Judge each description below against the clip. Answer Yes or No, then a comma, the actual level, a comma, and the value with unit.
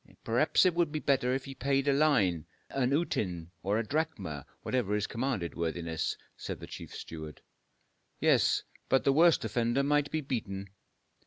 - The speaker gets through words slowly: No, average, 165 wpm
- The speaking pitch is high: No, low, 125 Hz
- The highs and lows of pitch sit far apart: Yes, wide, 7.1 semitones